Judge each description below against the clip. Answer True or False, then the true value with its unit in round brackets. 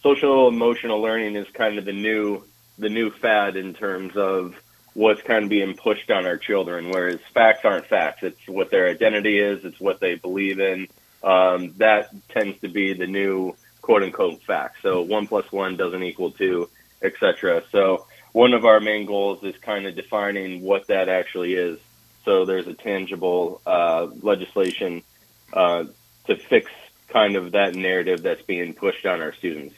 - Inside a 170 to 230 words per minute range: True (175 wpm)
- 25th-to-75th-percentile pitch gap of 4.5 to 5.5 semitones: False (3.3 semitones)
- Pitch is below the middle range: True (100 Hz)